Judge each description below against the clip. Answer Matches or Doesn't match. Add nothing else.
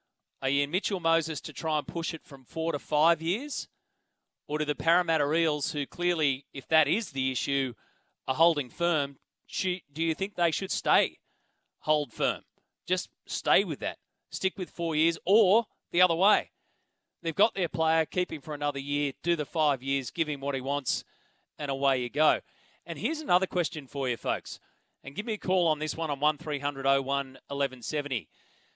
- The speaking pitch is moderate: Matches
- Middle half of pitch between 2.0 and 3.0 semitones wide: Doesn't match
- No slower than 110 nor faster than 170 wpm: Doesn't match